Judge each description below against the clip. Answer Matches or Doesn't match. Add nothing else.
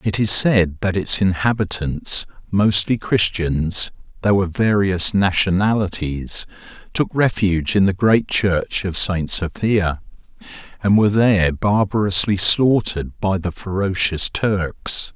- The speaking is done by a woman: Doesn't match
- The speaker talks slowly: Matches